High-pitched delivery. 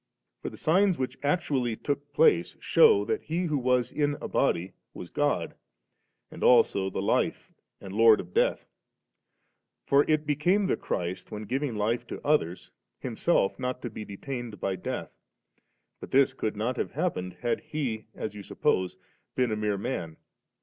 No: low, 125 Hz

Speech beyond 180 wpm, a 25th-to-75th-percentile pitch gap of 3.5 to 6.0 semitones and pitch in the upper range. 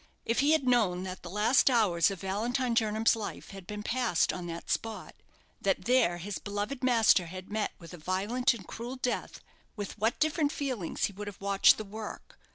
Yes: average, 195 wpm; average, 4.4 semitones; high, 210 Hz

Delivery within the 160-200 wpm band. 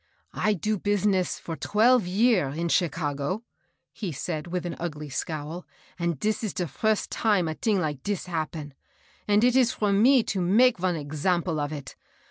Yes: average, 175 wpm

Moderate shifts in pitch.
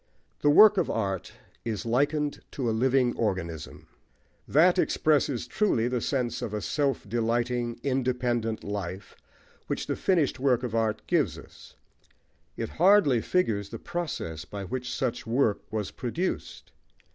Yes: average, 4.5 semitones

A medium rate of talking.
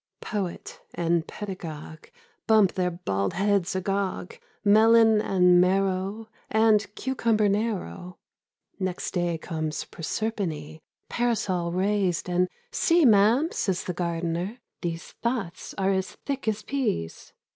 No: slow, 125 wpm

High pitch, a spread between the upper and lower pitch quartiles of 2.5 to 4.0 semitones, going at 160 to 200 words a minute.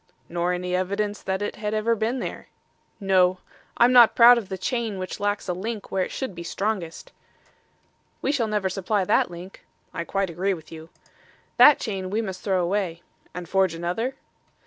Yes: high, 195 Hz; average, 3.1 semitones; average, 185 wpm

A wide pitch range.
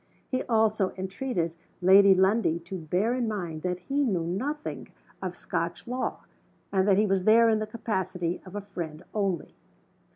No: average, 3.6 semitones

